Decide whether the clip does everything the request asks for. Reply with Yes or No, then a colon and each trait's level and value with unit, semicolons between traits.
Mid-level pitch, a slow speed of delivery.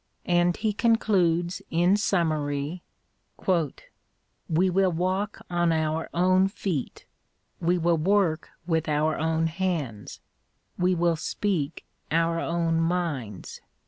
Yes: medium, 170 Hz; slow, 110 wpm